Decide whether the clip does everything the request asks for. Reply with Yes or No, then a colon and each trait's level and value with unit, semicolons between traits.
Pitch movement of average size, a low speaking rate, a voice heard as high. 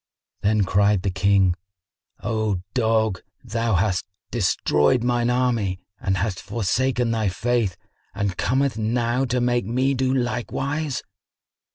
No: average, 3.7 semitones; slow, 125 wpm; low, 115 Hz